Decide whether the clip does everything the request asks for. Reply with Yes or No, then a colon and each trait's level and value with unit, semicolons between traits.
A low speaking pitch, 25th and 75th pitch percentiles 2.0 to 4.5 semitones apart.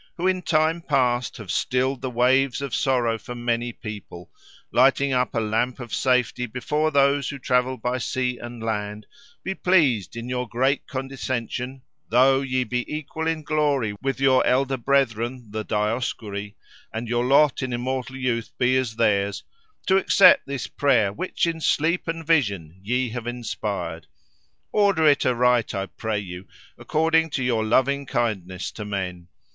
Yes: low, 125 Hz; average, 3.5 semitones